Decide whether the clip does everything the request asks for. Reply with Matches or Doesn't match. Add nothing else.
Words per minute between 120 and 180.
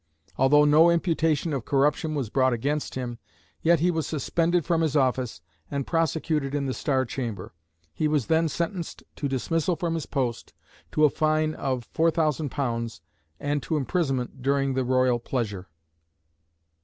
Matches